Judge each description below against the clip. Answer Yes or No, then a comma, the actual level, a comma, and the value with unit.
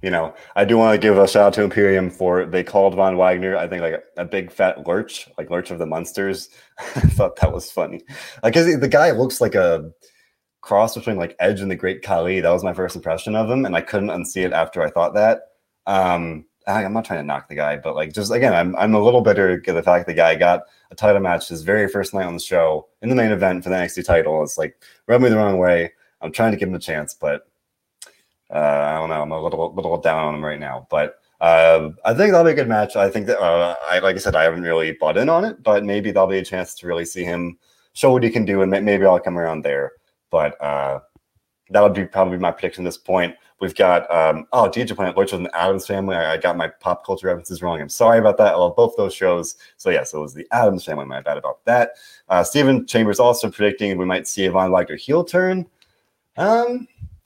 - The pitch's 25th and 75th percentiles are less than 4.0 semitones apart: No, average, 4.3 semitones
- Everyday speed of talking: No, fast, 260 wpm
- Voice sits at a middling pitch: No, very low, 95 Hz